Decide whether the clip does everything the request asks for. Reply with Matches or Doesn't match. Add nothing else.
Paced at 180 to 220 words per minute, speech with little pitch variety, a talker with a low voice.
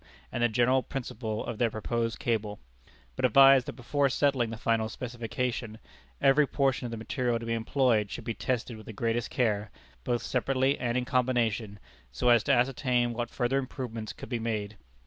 Matches